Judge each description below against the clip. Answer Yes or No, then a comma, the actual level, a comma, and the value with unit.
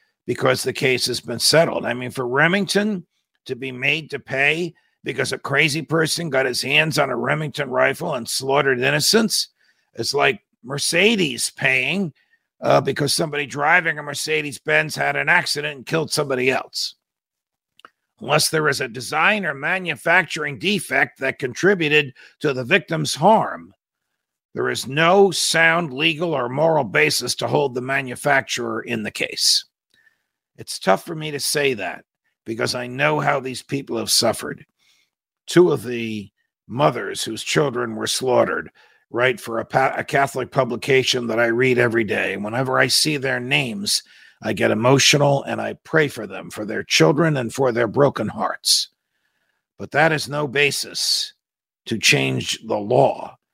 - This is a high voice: No, medium, 145 Hz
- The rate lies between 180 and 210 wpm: No, average, 160 wpm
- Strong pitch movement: No, average, 3.9 semitones